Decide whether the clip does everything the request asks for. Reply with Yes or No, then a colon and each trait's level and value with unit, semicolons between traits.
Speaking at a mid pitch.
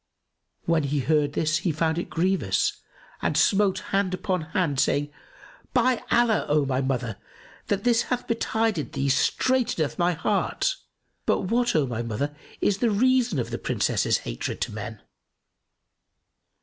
Yes: medium, 175 Hz